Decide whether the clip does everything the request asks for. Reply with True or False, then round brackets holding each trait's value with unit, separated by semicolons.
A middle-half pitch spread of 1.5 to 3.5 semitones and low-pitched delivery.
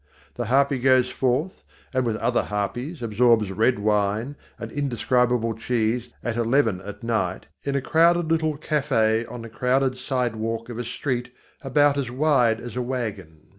True (3.1 semitones; 125 Hz)